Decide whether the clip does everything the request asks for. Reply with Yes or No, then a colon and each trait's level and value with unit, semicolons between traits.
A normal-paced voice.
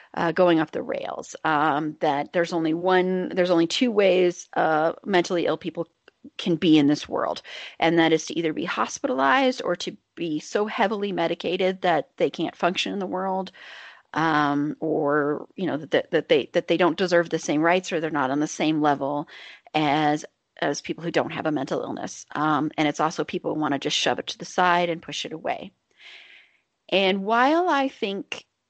Yes: average, 195 wpm